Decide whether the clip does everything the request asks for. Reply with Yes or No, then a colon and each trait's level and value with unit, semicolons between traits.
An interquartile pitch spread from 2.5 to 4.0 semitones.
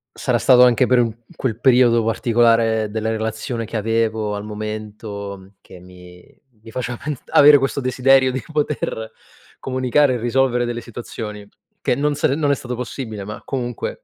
Yes: average, 2.9 semitones